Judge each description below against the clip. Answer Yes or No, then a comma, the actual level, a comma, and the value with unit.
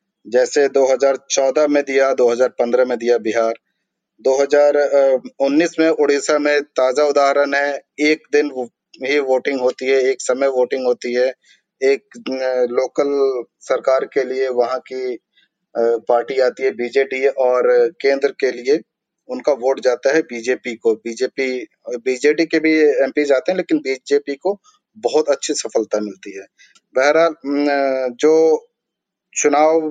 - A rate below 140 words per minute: Yes, average, 130 wpm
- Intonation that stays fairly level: No, average, 3.0 semitones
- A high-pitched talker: No, medium, 140 Hz